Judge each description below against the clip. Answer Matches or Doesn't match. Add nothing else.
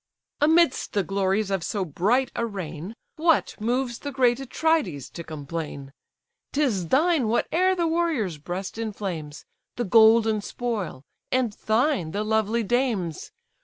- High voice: Matches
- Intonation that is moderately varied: Doesn't match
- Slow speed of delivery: Matches